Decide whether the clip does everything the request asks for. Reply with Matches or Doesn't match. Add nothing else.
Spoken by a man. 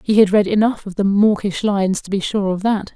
Doesn't match